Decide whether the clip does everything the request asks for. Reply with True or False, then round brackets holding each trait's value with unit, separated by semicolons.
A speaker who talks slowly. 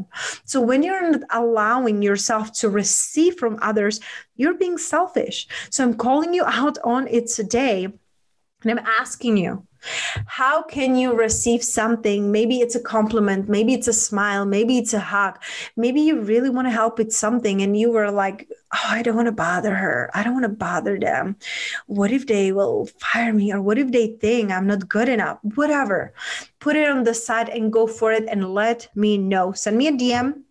False (195 wpm)